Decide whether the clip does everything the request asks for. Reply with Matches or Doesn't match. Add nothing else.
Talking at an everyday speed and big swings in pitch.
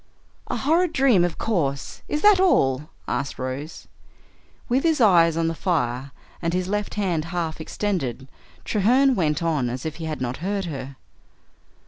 Matches